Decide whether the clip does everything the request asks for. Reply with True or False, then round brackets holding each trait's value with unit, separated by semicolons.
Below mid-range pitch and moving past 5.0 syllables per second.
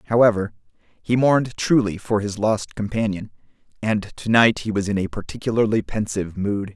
True (110 Hz; 5.3 syllables/s)